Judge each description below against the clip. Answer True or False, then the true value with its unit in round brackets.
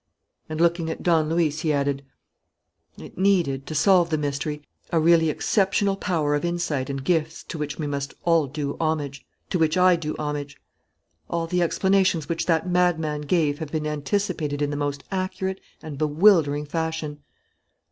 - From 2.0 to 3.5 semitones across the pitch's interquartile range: True (2.9 semitones)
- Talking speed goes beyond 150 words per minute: True (165 wpm)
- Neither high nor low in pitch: True (160 Hz)